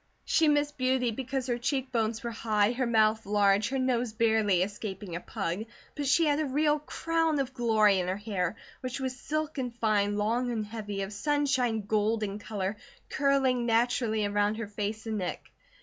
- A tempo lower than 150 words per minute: No, average, 180 wpm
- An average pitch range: Yes, average, 4.0 semitones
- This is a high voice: Yes, high, 225 Hz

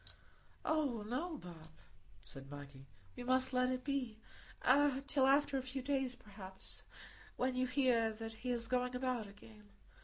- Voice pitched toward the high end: Yes, very high, 250 Hz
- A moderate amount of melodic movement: Yes, average, 3.5 semitones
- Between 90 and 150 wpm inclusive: Yes, average, 145 wpm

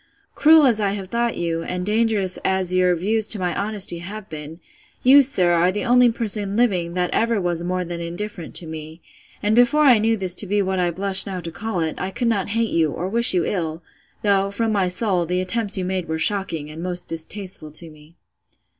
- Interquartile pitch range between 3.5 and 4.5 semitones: Yes, average, 3.8 semitones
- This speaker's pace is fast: Yes, fast, 220 wpm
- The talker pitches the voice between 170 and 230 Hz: Yes, high, 190 Hz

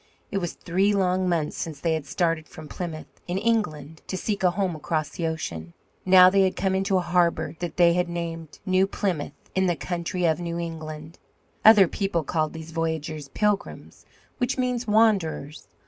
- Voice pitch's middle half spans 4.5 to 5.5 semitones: No, average, 3.0 semitones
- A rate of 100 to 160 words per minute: No, average, 180 wpm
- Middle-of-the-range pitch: Yes, medium, 175 Hz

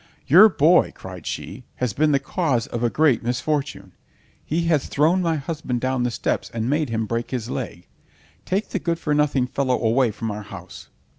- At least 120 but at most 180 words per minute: No, average, 195 wpm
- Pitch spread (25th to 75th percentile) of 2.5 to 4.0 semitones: No, average, 4.9 semitones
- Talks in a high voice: No, low, 130 Hz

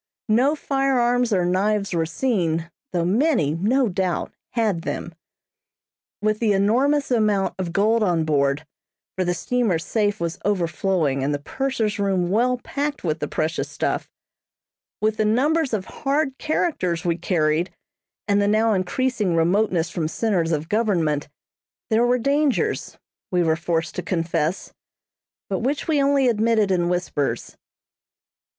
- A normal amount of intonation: No, wide, 6.0 semitones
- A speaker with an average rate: Yes, average, 145 wpm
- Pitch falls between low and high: No, high, 200 Hz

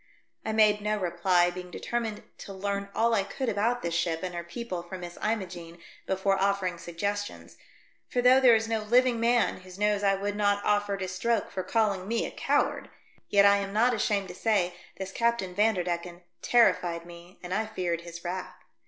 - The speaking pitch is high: Yes, high, 200 Hz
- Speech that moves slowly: No, average, 195 wpm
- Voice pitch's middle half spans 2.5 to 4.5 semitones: Yes, average, 3.5 semitones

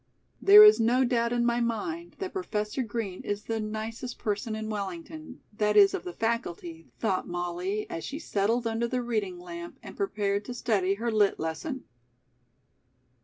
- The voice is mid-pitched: No, high, 220 Hz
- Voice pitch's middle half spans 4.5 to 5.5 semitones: No, average, 3.4 semitones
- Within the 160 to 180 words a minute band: Yes, average, 170 wpm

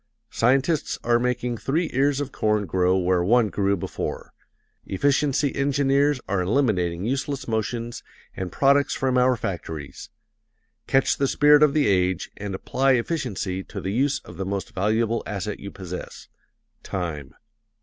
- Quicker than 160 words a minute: No, average, 145 wpm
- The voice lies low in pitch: Yes, low, 115 Hz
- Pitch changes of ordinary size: No, wide, 6.2 semitones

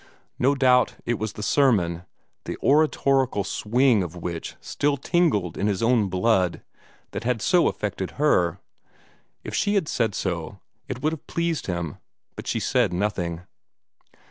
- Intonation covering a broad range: Yes, wide, 7.1 semitones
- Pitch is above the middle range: No, low, 110 Hz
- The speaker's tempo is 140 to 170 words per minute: Yes, average, 150 wpm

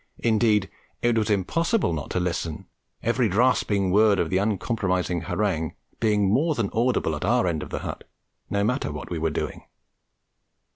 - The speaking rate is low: No, average, 165 wpm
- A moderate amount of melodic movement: Yes, average, 4.4 semitones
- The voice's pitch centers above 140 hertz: No, low, 105 Hz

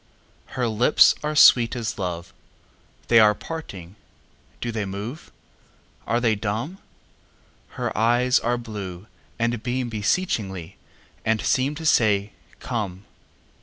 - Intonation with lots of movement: No, average, 3.3 semitones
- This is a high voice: No, low, 115 Hz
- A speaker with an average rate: No, slow, 95 wpm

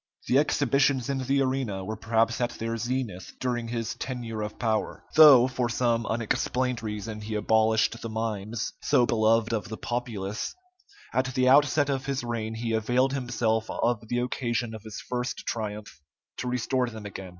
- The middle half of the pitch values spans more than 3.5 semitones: No, narrow, 2.4 semitones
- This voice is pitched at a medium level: No, low, 115 Hz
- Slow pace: No, average, 170 wpm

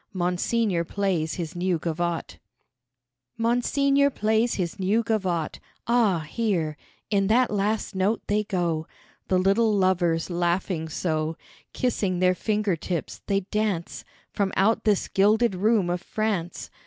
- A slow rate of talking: Yes, slow, 130 wpm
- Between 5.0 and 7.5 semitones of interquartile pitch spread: No, average, 3.8 semitones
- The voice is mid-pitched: No, high, 195 Hz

